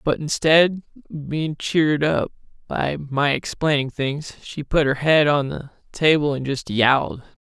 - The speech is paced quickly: No, average, 160 wpm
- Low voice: No, medium, 145 Hz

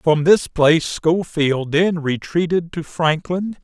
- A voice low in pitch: No, medium, 165 Hz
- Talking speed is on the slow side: Yes, slow, 130 wpm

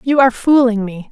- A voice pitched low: No, high, 240 Hz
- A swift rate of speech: Yes, fast, 215 wpm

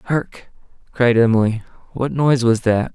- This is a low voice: Yes, low, 120 Hz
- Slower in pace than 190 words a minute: Yes, average, 140 wpm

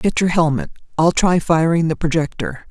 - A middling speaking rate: Yes, average, 180 wpm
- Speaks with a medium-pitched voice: Yes, medium, 165 Hz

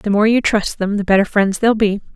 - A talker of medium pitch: No, high, 205 Hz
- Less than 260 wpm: No, fast, 280 wpm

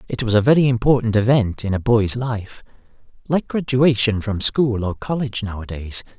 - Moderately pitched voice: No, low, 115 Hz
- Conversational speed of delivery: Yes, average, 165 wpm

